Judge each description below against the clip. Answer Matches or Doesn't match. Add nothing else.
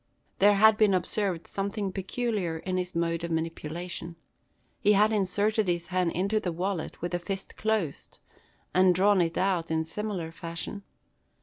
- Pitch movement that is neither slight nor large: Matches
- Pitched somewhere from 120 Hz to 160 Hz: Doesn't match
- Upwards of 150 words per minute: Matches